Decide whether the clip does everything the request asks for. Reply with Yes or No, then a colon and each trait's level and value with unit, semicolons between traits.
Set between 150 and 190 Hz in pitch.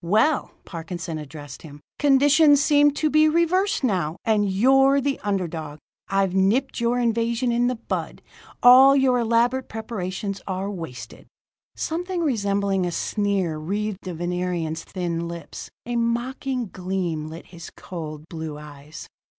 No: high, 200 Hz